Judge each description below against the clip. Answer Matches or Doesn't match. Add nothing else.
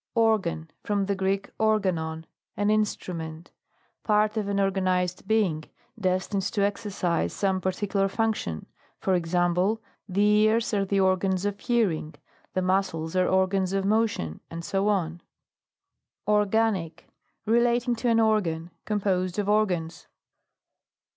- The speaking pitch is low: Doesn't match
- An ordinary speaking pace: Doesn't match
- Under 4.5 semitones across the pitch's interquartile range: Matches